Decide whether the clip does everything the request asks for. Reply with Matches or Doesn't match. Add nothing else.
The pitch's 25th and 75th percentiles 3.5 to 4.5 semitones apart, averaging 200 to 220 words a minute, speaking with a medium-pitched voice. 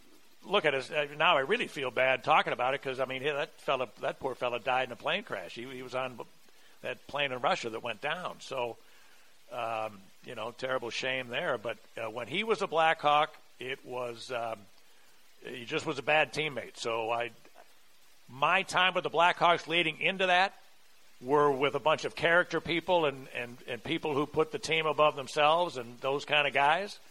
Matches